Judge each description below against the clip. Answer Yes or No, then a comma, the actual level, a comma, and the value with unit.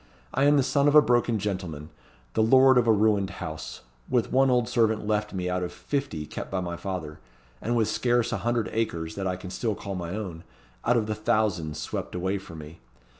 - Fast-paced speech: Yes, fast, 220 wpm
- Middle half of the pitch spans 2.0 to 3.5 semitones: No, average, 4.7 semitones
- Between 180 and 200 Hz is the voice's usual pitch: No, low, 105 Hz